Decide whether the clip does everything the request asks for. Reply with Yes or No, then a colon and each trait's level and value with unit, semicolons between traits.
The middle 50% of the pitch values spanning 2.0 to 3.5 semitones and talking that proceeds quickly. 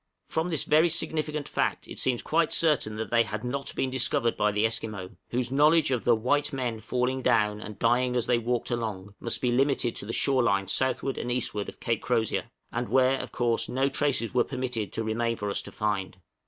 Yes: average, 3.1 semitones; fast, 215 wpm